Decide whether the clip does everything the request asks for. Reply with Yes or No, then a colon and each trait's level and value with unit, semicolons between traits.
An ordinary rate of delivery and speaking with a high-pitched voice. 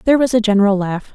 No: fast, 265 wpm; high, 215 Hz